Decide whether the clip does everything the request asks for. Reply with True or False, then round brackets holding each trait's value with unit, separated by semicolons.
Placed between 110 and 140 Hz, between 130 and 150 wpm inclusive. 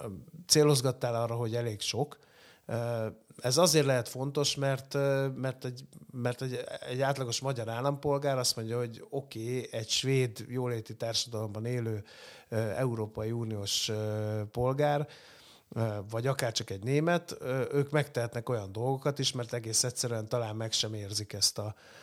True (120 Hz; 135 wpm)